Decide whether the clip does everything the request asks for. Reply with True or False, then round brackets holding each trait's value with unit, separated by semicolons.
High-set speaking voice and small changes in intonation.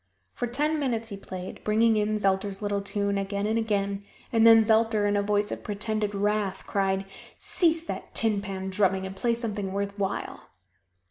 True (205 Hz; 2.1 semitones)